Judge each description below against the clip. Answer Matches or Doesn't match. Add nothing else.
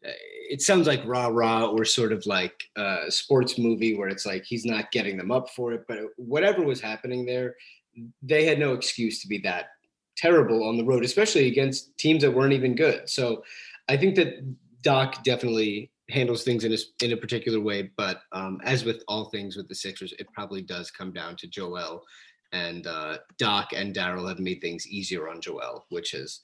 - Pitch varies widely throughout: Doesn't match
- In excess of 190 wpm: Matches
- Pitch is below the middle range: Matches